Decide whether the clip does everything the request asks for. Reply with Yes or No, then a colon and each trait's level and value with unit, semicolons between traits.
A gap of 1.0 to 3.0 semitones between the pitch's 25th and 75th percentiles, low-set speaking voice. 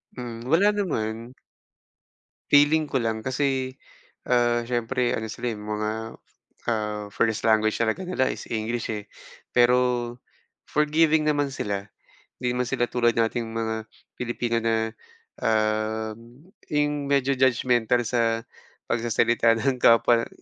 Yes: narrow, 2.6 semitones; low, 120 Hz